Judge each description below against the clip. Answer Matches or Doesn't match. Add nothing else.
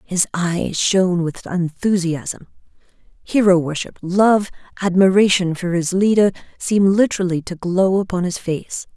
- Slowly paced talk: Matches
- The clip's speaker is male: Doesn't match